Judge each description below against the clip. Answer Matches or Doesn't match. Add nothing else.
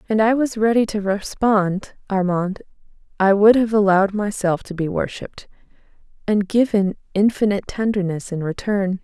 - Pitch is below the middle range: Doesn't match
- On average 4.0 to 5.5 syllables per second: Matches